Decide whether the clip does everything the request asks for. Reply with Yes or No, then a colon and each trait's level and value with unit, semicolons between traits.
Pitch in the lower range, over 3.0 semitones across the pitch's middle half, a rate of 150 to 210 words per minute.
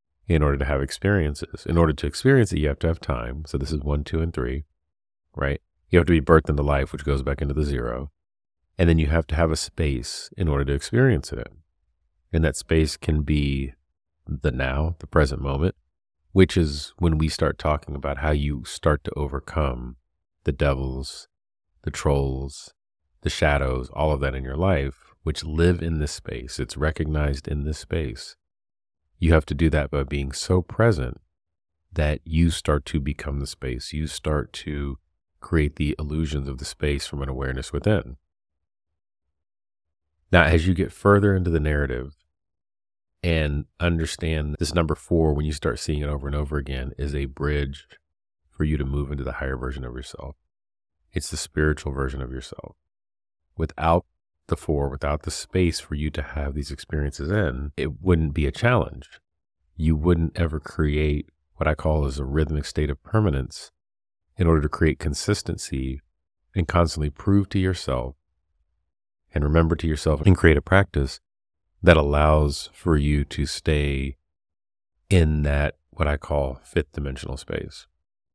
No: very low, 75 Hz; narrow, 2.6 semitones; average, 175 wpm